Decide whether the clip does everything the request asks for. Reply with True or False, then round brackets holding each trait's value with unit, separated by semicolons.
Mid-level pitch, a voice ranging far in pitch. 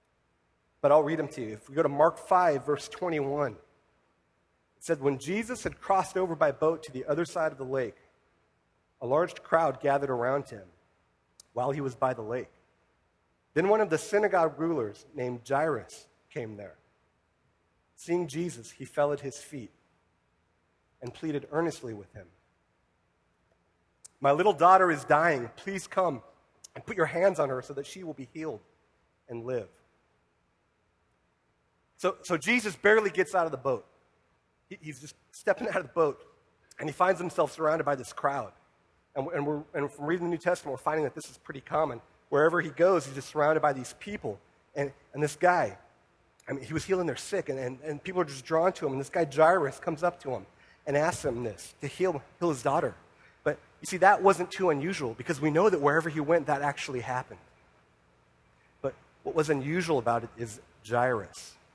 True (145 Hz; 6.3 semitones)